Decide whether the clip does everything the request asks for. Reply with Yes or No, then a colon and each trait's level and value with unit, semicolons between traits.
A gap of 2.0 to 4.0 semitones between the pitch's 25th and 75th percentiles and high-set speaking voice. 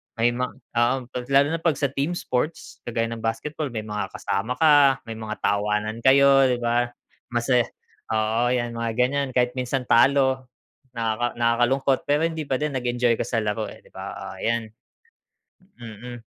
No: average, 2.9 semitones; low, 120 Hz